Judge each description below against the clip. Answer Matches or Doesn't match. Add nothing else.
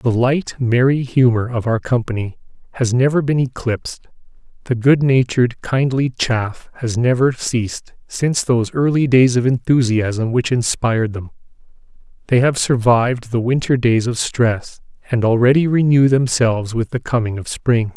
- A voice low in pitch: Matches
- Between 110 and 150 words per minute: Matches